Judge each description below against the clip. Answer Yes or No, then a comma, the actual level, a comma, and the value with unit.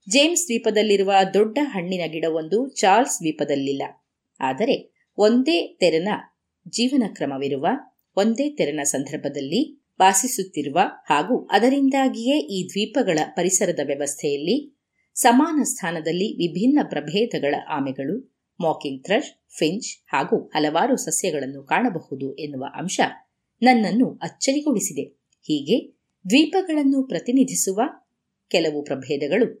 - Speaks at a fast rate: No, average, 85 wpm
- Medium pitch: No, high, 195 Hz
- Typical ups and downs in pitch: No, wide, 8.8 semitones